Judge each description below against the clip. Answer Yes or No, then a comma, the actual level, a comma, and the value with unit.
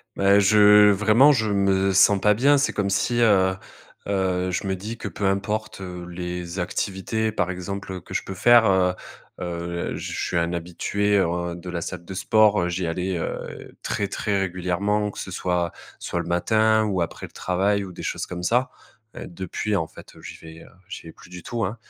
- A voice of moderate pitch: No, very low, 95 Hz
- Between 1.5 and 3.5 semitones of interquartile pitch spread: Yes, average, 2.9 semitones